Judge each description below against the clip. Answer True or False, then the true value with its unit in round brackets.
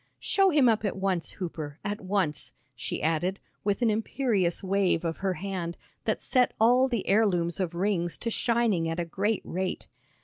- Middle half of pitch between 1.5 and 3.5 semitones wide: False (4.3 semitones)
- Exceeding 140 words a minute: True (175 wpm)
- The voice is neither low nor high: False (195 Hz)